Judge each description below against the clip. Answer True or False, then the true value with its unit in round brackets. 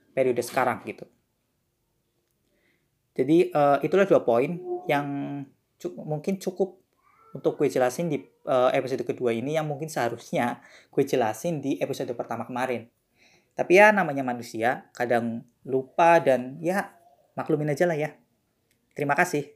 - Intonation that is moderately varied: False (5.7 semitones)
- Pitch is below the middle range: False (145 Hz)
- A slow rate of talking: False (130 wpm)